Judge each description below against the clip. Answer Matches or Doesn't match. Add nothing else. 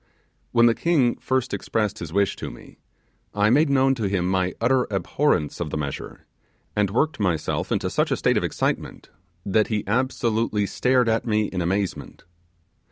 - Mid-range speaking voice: Doesn't match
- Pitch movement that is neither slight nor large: Matches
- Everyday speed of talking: Matches